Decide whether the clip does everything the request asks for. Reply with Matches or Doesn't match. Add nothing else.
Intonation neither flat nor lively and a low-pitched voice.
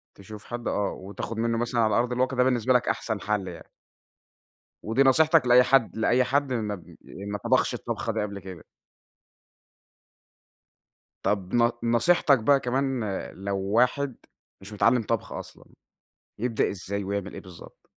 Matches